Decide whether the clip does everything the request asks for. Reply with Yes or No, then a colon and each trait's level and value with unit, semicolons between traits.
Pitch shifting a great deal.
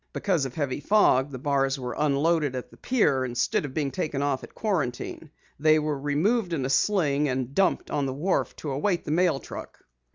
No: average, 3.6 semitones